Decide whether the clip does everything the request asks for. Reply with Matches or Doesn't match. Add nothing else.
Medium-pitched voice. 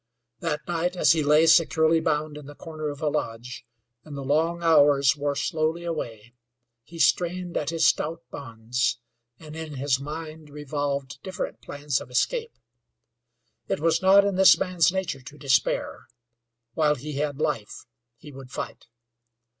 Matches